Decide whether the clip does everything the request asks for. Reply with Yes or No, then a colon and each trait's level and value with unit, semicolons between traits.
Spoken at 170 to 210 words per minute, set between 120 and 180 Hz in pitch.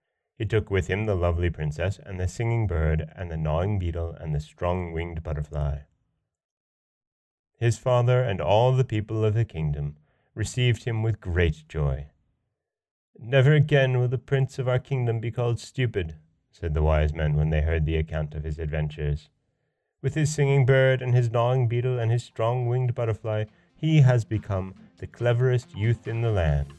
No: average, 175 wpm; low, 105 Hz